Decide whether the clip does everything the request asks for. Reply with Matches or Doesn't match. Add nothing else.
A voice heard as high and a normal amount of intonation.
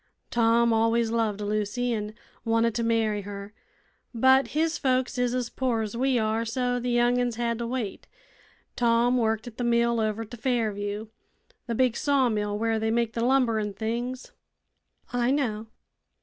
Doesn't match